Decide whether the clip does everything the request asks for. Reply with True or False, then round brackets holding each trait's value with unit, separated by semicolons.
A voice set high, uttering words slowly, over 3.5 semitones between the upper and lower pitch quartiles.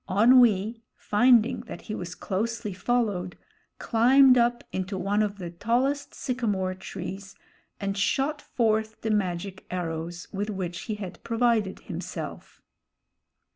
True (210 Hz; 125 wpm; 4.0 semitones)